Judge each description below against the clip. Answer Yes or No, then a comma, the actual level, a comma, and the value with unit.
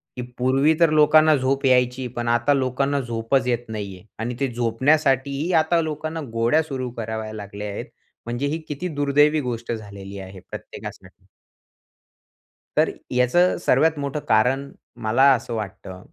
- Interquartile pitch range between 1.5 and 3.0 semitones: No, average, 4.2 semitones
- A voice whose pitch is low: Yes, low, 125 Hz